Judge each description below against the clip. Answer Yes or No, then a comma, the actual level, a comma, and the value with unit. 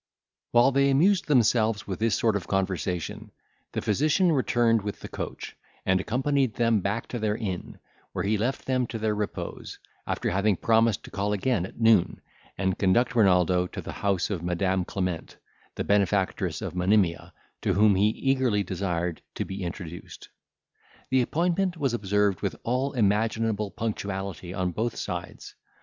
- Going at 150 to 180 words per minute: Yes, average, 160 wpm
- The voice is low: Yes, low, 105 Hz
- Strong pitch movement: No, average, 4.0 semitones